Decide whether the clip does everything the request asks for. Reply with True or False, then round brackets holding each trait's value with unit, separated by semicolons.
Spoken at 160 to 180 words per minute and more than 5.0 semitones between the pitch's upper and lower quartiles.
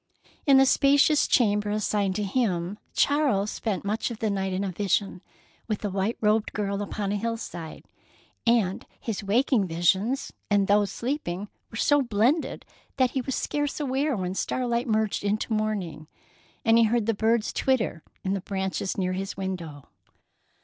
False (165 wpm; 3.5 semitones)